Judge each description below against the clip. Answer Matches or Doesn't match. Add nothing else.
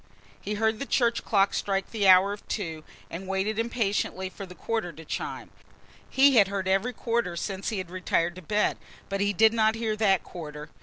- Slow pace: Doesn't match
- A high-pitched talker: Matches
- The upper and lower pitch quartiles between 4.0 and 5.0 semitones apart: Doesn't match